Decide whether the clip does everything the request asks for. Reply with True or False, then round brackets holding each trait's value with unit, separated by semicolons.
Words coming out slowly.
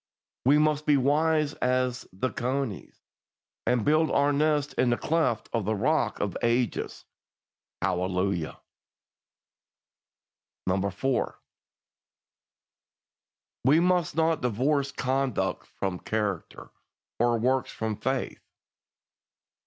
True (100 wpm)